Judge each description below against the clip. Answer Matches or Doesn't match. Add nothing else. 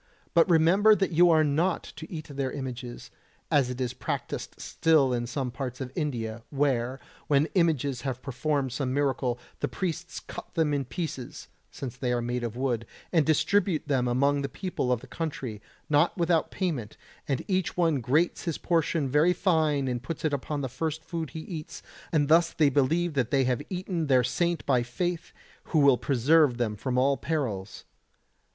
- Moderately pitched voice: Matches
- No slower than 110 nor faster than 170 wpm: Doesn't match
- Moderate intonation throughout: Matches